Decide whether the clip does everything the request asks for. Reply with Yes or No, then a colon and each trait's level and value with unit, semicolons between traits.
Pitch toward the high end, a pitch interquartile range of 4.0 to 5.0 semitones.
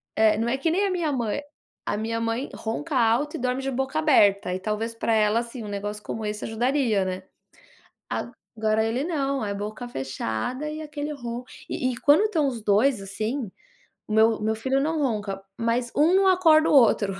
Yes: high, 235 Hz; average, 4.7 semitones